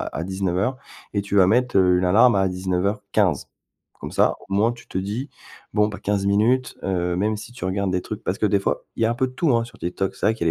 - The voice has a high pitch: No, low, 100 Hz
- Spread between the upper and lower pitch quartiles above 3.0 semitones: Yes, average, 3.5 semitones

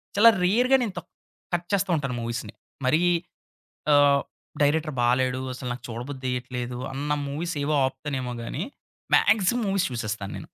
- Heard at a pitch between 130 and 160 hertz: Yes, medium, 140 Hz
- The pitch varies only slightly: No, wide, 5.6 semitones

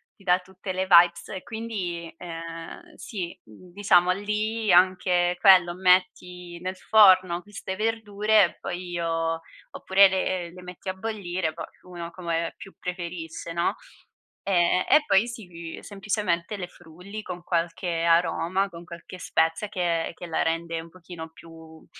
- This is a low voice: No, medium, 180 Hz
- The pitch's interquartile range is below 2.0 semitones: No, narrow, 2.3 semitones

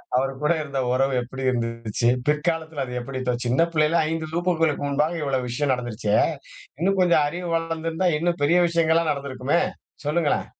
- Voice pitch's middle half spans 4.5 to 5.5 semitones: No, average, 4.0 semitones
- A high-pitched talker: No, medium, 150 Hz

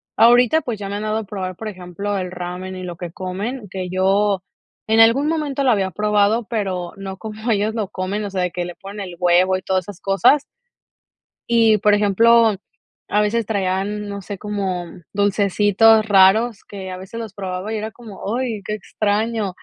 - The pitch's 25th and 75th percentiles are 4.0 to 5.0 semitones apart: No, average, 2.7 semitones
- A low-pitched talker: No, high, 205 Hz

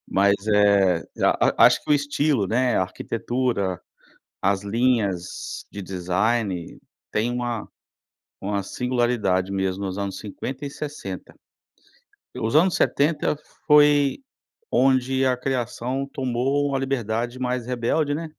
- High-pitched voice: No, low, 120 Hz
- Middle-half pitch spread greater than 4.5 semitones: Yes, average, 5.0 semitones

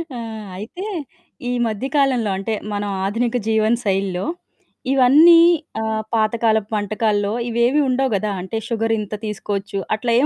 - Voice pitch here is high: Yes, high, 220 Hz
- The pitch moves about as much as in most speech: Yes, average, 3.0 semitones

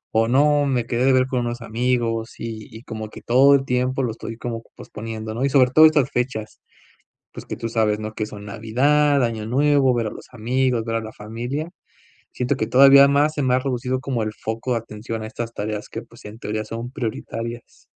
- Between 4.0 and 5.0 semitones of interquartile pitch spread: No, average, 2.8 semitones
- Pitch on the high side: No, low, 120 Hz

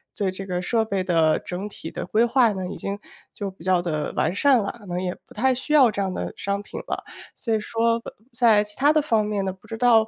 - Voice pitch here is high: Yes, high, 205 Hz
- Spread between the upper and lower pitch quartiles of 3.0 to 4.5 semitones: Yes, average, 3.7 semitones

